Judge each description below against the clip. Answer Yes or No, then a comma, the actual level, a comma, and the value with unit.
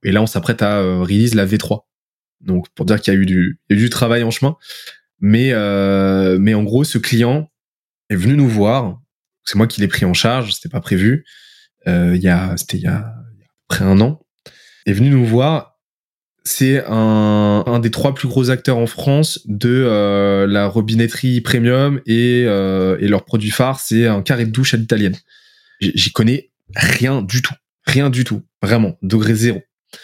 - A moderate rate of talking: Yes, average, 195 wpm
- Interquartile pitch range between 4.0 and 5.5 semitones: Yes, average, 4.4 semitones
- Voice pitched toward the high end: No, low, 115 Hz